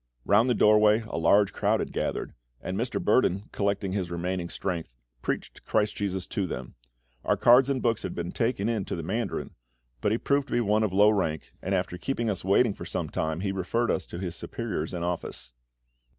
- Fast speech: Yes, fast, 210 wpm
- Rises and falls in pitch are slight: No, average, 4.0 semitones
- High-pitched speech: No, low, 100 Hz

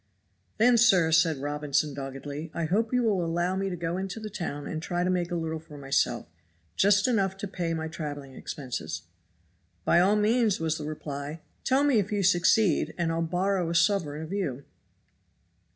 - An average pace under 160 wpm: No, average, 185 wpm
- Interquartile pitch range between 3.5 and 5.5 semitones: Yes, average, 4.3 semitones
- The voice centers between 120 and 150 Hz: No, medium, 170 Hz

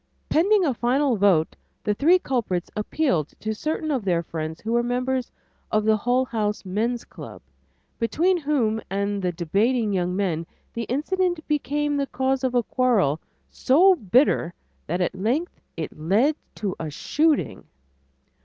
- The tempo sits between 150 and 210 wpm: Yes, average, 155 wpm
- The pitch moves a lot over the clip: Yes, wide, 6.6 semitones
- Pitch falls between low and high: No, high, 235 Hz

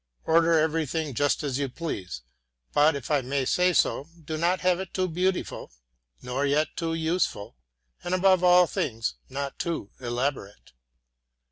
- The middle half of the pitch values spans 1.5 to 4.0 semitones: No, average, 4.4 semitones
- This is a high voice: No, medium, 155 Hz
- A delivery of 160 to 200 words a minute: No, average, 150 wpm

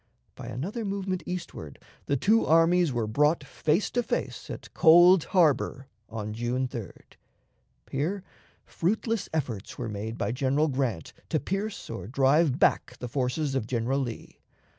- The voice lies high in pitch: No, medium, 140 Hz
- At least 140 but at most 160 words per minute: Yes, average, 145 wpm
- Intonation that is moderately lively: No, wide, 6.7 semitones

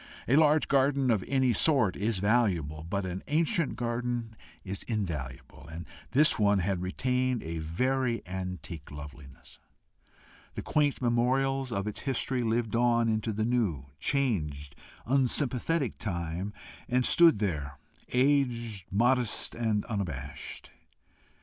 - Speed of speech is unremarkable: No, slow, 125 wpm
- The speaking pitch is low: Yes, low, 115 Hz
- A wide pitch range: Yes, wide, 5.9 semitones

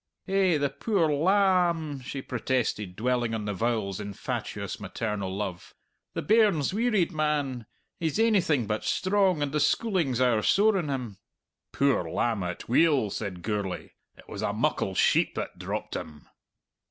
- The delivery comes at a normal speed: Yes, average, 155 wpm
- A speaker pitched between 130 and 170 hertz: Yes, low, 135 Hz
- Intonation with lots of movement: Yes, wide, 8.6 semitones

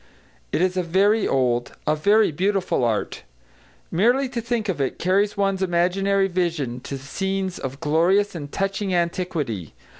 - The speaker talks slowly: No, average, 150 wpm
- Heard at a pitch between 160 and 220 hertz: Yes, medium, 185 Hz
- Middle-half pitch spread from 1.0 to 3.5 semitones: No, average, 4.7 semitones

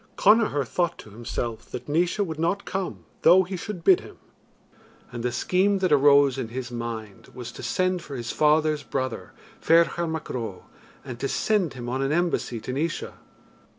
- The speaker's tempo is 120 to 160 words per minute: No, average, 180 wpm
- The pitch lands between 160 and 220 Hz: No, medium, 150 Hz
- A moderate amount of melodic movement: No, wide, 6.2 semitones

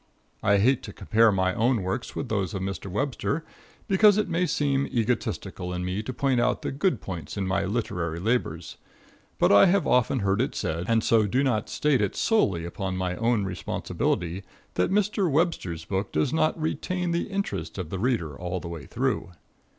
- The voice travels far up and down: Yes, wide, 6.9 semitones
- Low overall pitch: Yes, low, 105 Hz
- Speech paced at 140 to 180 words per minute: No, average, 190 wpm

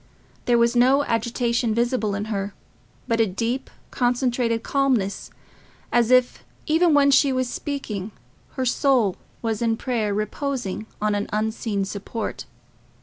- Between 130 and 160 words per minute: Yes, slow, 135 wpm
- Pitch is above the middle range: Yes, high, 235 Hz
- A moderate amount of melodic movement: Yes, average, 3.3 semitones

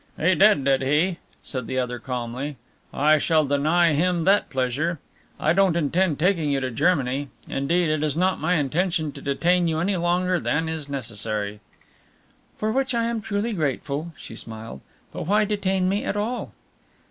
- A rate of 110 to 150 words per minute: No, average, 170 wpm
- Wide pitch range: No, average, 4.9 semitones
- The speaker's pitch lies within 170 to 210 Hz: No, medium, 160 Hz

